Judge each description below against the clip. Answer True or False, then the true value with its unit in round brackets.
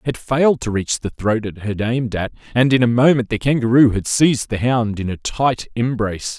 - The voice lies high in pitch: False (120 Hz)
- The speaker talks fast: True (225 wpm)